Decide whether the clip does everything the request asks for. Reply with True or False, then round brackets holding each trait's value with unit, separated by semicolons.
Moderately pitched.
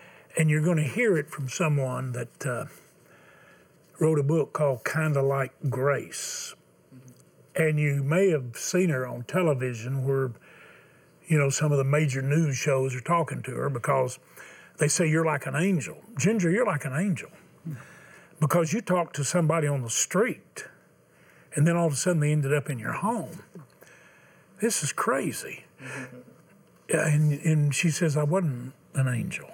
True (150 Hz)